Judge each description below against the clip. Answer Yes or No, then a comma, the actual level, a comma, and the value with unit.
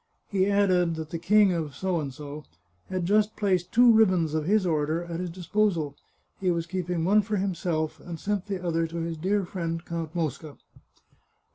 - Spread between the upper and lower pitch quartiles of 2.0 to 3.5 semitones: Yes, average, 3.2 semitones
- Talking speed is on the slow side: No, average, 170 wpm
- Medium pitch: Yes, medium, 175 Hz